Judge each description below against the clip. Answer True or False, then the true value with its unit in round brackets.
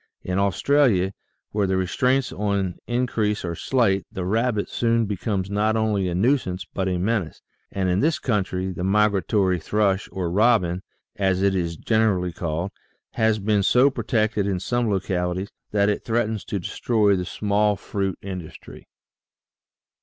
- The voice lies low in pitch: True (100 Hz)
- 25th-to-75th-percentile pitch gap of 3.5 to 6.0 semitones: False (2.9 semitones)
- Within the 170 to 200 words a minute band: False (155 wpm)